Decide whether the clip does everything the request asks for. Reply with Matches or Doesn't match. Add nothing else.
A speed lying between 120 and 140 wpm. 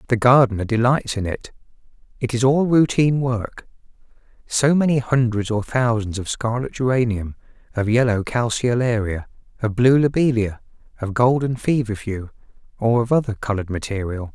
Matches